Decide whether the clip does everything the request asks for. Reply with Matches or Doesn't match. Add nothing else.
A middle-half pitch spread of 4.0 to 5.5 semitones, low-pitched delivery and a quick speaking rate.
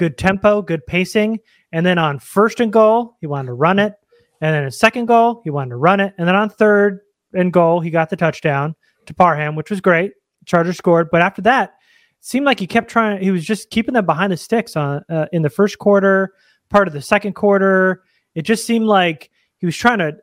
Doesn't match